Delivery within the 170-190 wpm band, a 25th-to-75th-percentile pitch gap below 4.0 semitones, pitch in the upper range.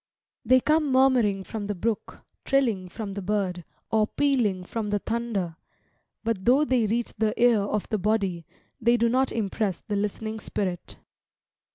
No: average, 160 wpm; average, 3.0 semitones; high, 215 Hz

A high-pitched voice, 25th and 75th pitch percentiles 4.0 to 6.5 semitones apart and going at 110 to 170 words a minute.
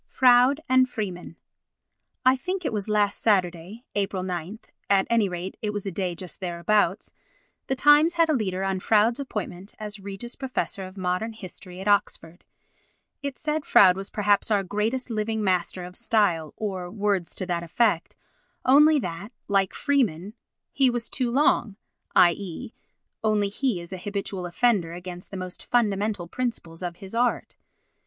Yes: high, 205 Hz; average, 4.5 semitones; average, 160 wpm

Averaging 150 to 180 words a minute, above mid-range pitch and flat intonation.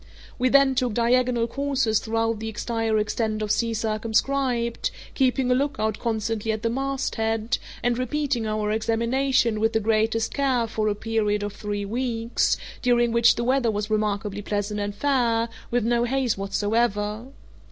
Yes: average, 155 wpm; high, 225 Hz; narrow, 2.3 semitones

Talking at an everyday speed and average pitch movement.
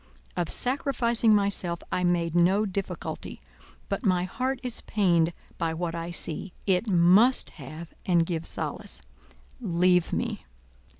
No: slow, 130 wpm; average, 3.7 semitones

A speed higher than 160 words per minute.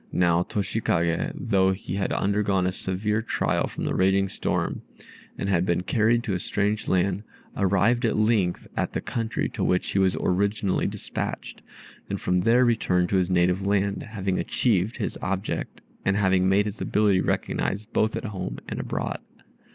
Yes: average, 170 wpm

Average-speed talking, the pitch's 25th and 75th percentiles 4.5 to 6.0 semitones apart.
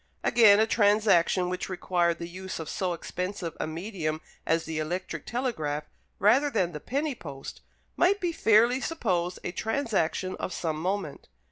Yes: average, 155 wpm; average, 5.0 semitones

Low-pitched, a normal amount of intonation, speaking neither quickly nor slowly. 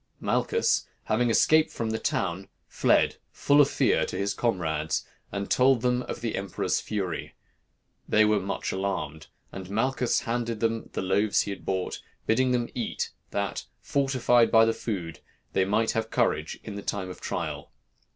Yes: low, 110 Hz; average, 3.8 semitones; average, 165 wpm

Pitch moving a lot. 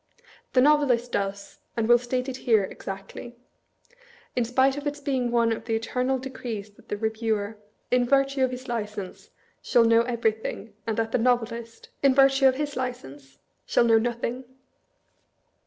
No: average, 2.7 semitones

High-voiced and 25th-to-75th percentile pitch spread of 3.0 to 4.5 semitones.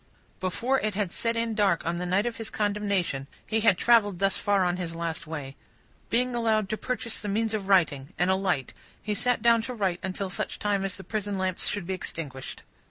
Yes: high, 200 Hz; average, 3.5 semitones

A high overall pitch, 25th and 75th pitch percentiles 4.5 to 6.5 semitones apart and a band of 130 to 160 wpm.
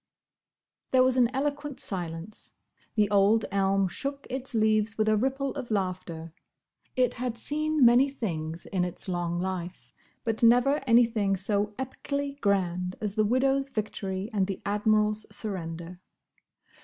Yes: high, 215 Hz; average, 5.1 semitones; average, 140 wpm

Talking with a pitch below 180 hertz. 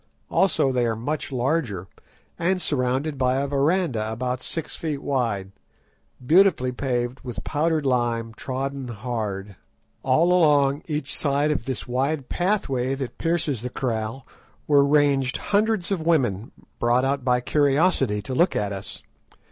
Yes: low, 135 Hz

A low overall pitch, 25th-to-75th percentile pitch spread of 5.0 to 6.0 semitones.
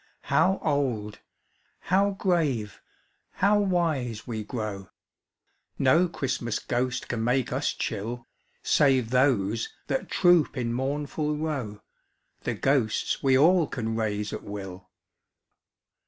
Yes: low, 130 Hz; average, 5.3 semitones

